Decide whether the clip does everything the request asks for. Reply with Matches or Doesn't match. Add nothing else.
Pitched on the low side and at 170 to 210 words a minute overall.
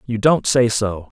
Matches